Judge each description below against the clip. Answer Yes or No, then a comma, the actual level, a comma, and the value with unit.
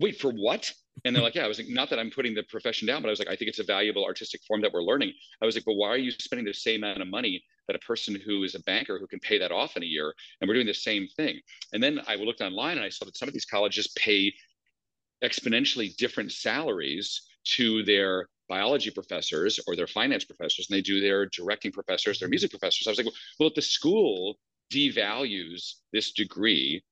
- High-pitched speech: No, low, 130 Hz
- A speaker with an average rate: No, fast, 245 wpm